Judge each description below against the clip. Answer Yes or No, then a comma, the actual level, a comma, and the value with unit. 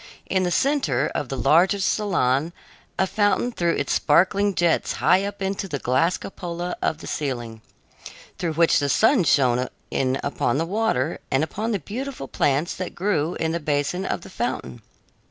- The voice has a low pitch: No, medium, 170 Hz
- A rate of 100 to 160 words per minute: No, average, 175 wpm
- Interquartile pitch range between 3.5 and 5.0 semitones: No, wide, 5.6 semitones